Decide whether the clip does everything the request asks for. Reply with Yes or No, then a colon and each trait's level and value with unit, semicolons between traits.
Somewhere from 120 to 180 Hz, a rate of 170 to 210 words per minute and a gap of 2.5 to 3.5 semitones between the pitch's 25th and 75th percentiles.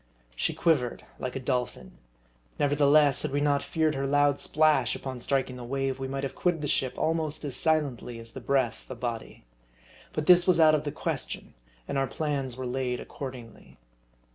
Yes: low, 135 Hz; average, 190 wpm; average, 2.9 semitones